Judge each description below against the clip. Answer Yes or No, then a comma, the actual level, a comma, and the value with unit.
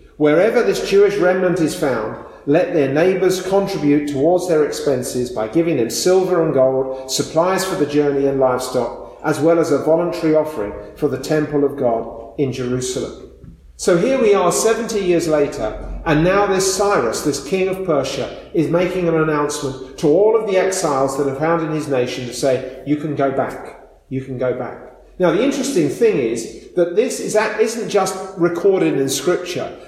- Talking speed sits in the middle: Yes, average, 185 wpm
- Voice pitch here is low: No, medium, 155 Hz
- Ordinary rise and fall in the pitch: No, wide, 5.7 semitones